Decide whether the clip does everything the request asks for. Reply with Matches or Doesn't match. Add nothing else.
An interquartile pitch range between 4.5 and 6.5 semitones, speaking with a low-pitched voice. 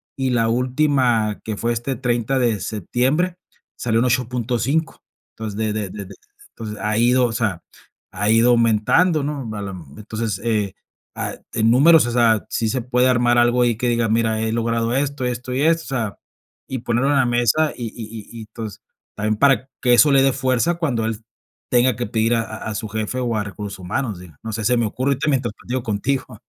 Doesn't match